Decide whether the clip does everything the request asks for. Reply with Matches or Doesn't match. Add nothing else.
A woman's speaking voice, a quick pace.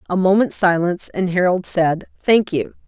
Doesn't match